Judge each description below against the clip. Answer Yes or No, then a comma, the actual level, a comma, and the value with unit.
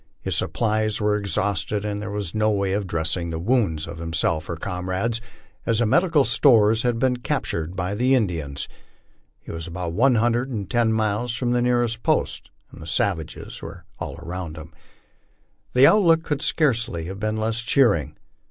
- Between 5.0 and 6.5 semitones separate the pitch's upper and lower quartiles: Yes, wide, 5.4 semitones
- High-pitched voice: No, low, 105 Hz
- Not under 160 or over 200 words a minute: Yes, average, 170 wpm